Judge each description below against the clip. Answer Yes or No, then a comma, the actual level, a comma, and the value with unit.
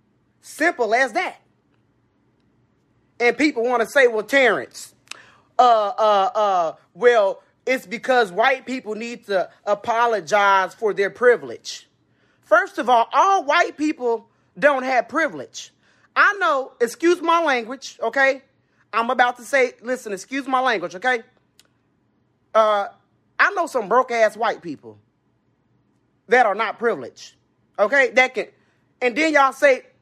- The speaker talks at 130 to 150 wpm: Yes, slow, 135 wpm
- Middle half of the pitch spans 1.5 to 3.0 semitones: No, average, 4.0 semitones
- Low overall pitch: No, high, 245 Hz